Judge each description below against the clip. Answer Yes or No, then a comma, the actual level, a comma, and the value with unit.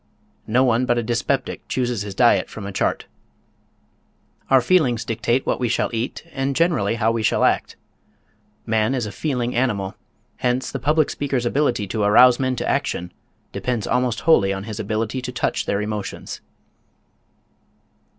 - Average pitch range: Yes, average, 3.1 semitones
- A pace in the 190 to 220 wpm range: No, average, 160 wpm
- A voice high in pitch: No, low, 120 Hz